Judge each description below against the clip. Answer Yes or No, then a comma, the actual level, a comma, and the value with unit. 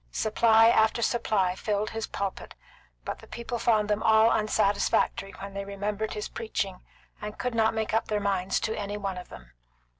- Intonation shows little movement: Yes, narrow, 1.9 semitones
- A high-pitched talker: Yes, high, 210 Hz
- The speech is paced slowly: No, average, 180 wpm